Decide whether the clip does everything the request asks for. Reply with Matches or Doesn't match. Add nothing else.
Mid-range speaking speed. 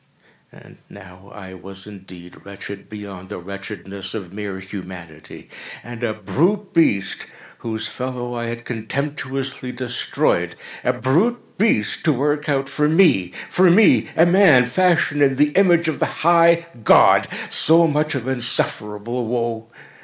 Doesn't match